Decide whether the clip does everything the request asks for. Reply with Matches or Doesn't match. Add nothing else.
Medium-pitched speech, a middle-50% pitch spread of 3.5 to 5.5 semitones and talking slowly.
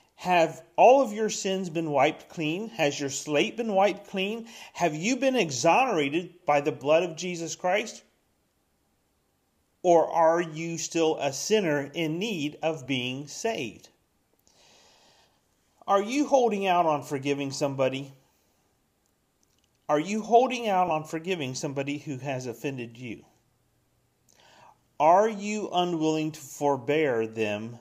Matches